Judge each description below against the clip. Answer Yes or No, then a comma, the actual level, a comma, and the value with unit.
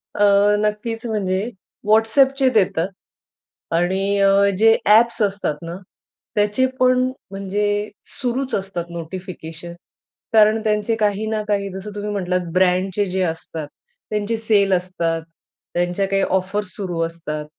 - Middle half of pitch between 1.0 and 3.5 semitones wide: Yes, average, 2.8 semitones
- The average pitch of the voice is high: Yes, high, 200 Hz